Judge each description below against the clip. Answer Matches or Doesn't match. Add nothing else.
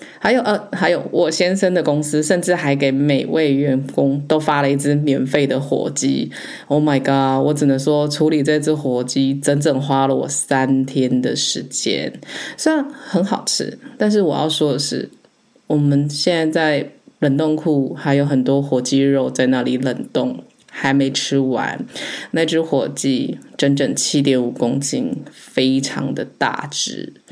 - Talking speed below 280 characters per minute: Matches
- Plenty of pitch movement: Doesn't match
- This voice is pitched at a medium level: Matches